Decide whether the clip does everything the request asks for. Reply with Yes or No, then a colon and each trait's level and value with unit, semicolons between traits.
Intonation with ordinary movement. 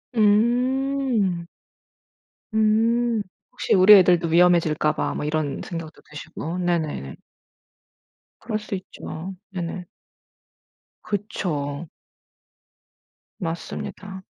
Yes: average, 4.6 semitones